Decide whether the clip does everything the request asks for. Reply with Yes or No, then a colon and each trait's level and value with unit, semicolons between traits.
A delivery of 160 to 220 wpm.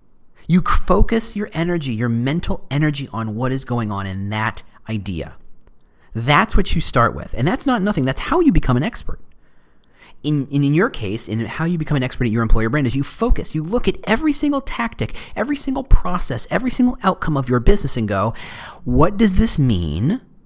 Yes: average, 200 wpm